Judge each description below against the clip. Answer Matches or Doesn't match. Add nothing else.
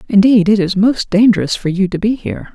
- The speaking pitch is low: Doesn't match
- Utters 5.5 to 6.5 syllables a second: Matches